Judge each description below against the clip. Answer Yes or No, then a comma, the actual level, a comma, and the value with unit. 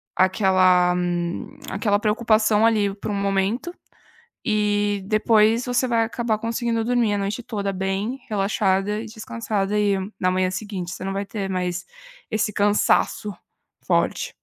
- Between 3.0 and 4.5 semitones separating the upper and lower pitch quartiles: No, narrow, 2.4 semitones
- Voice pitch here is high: Yes, high, 205 Hz